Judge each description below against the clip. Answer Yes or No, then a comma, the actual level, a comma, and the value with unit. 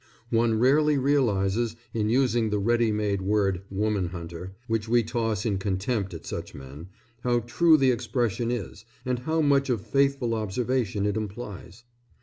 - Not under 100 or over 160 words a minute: Yes, average, 155 wpm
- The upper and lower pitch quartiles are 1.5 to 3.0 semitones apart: No, average, 3.8 semitones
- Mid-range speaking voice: No, low, 115 Hz